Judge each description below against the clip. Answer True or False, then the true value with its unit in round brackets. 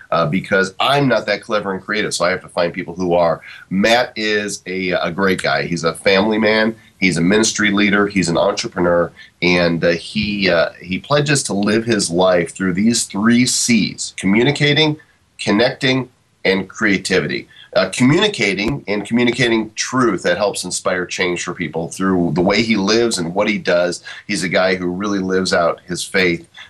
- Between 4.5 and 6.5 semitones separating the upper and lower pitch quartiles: False (3.9 semitones)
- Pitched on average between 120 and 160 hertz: False (100 Hz)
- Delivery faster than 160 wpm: True (180 wpm)